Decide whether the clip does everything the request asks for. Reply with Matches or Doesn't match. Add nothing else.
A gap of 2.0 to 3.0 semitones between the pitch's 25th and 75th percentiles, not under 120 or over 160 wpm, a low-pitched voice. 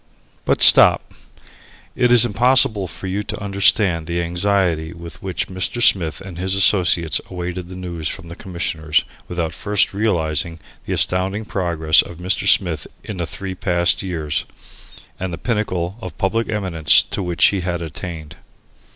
Matches